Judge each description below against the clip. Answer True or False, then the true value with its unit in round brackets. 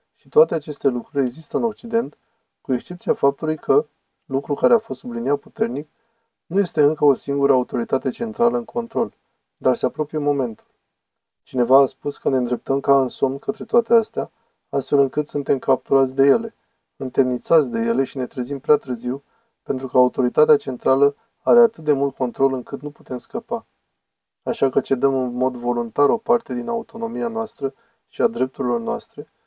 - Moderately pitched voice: True (145 Hz)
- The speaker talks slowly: False (170 wpm)